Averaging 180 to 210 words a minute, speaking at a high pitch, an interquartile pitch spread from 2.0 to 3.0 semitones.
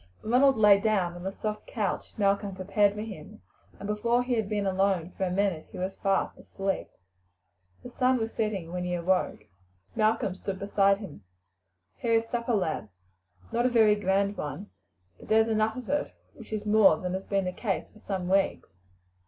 Yes: average, 185 wpm; high, 200 Hz; narrow, 2.6 semitones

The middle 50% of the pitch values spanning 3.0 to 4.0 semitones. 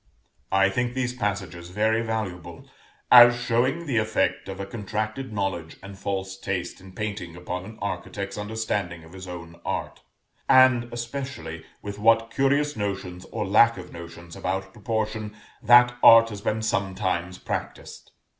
Yes: average, 3.6 semitones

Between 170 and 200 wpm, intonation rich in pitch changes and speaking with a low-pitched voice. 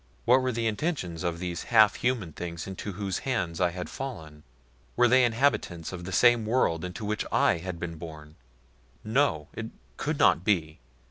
Yes: average, 180 wpm; wide, 5.9 semitones; very low, 95 Hz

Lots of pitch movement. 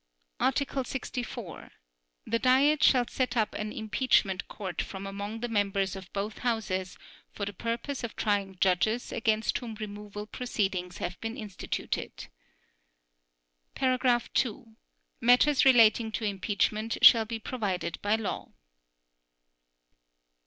No: average, 3.4 semitones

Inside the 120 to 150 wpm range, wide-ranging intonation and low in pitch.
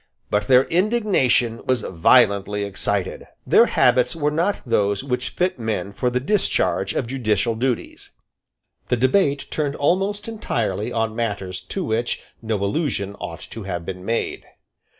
Yes: average, 145 wpm; wide, 5.8 semitones; low, 120 Hz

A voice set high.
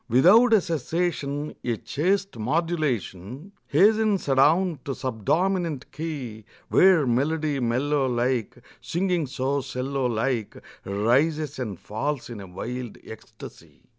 No: medium, 140 Hz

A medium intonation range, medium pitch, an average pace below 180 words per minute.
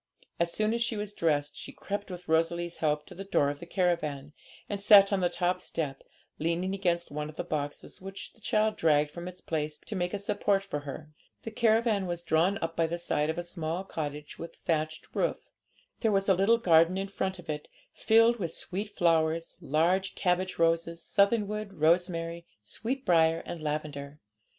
No: average, 3.8 semitones; medium, 175 Hz; average, 195 wpm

